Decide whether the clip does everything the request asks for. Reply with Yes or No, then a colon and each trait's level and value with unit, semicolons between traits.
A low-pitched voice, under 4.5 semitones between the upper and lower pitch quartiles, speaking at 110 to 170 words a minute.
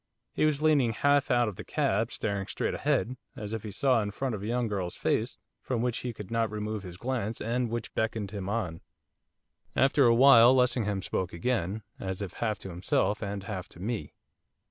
No: low, 110 Hz; average, 3.6 semitones; average, 200 wpm